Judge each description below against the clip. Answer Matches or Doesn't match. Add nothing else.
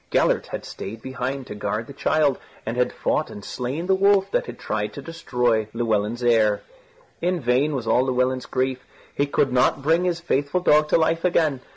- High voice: Doesn't match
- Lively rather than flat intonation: Doesn't match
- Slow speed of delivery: Doesn't match